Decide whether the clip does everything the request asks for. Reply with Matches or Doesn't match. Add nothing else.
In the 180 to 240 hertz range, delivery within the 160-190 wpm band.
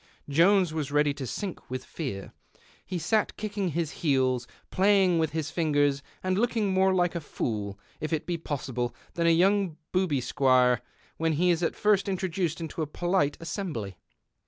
Doesn't match